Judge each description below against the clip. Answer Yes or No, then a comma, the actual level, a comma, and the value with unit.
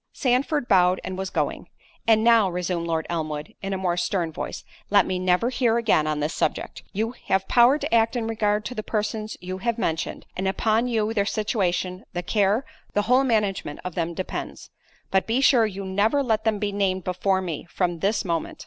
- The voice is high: Yes, high, 200 Hz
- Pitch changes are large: No, average, 3.7 semitones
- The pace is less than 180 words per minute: No, average, 200 wpm